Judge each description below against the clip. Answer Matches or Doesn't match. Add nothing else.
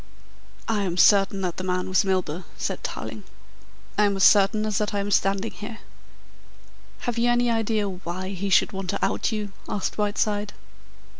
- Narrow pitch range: Matches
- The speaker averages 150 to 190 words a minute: Matches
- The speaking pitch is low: Doesn't match